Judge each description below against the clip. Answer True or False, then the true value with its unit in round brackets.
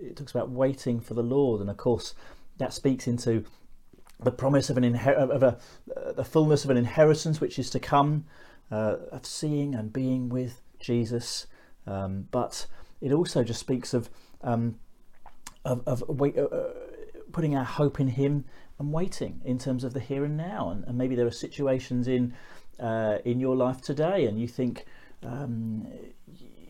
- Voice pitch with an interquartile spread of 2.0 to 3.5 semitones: True (3.1 semitones)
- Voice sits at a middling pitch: False (130 Hz)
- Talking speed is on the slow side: False (180 wpm)